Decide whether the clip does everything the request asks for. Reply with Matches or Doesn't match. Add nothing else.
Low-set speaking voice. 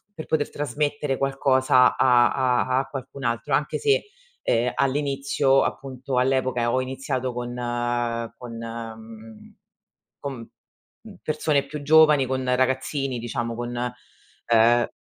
Matches